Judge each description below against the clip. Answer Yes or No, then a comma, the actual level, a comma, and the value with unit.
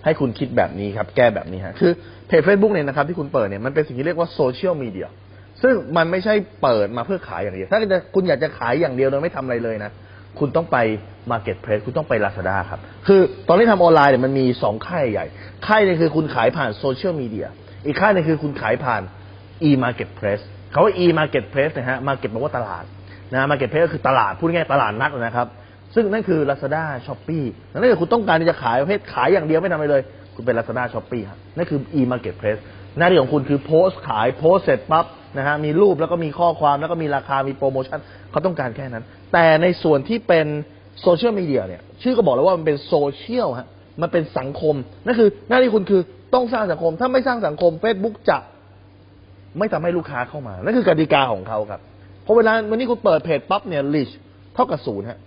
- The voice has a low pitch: No, medium, 145 Hz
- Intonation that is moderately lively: No, wide, 8.0 semitones